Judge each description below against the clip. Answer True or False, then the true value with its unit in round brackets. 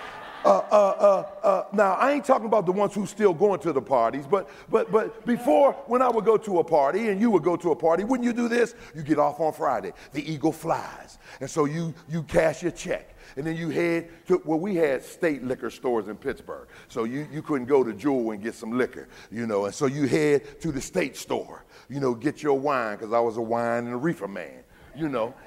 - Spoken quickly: True (245 wpm)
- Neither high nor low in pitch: True (165 Hz)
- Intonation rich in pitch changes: True (6.8 semitones)